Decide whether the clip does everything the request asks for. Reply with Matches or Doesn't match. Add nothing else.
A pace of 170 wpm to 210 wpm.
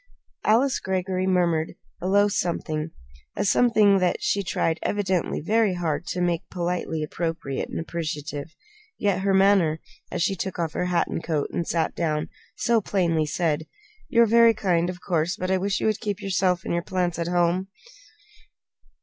Matches